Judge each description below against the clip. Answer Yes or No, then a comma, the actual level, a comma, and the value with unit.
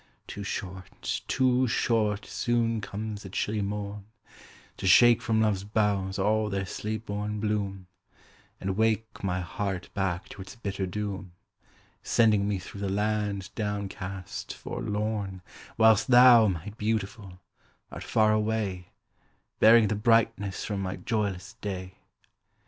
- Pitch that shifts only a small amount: Yes, narrow, 2.1 semitones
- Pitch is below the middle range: Yes, low, 105 Hz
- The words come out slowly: Yes, slow, 130 wpm